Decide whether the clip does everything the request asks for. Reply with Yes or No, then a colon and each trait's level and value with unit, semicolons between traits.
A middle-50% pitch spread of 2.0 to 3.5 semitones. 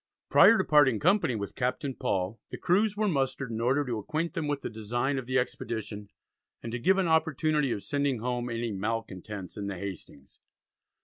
No: average, 5.3 semitones